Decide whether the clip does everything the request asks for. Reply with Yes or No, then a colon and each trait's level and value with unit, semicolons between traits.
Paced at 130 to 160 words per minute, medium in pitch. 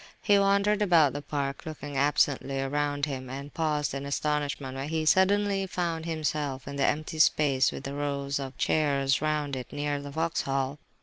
No: average, 175 wpm; medium, 145 Hz